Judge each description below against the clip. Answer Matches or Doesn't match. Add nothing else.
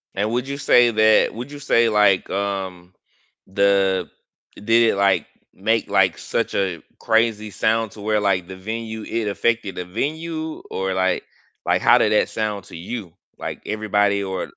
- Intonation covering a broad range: Doesn't match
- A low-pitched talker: Matches